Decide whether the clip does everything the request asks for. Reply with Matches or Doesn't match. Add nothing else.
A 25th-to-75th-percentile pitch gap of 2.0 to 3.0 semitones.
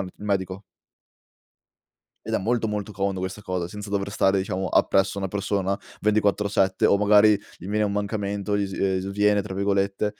Doesn't match